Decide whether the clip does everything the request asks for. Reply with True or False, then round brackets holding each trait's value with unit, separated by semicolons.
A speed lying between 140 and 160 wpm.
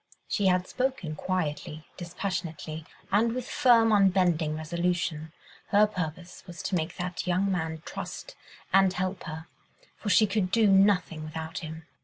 True (145 wpm)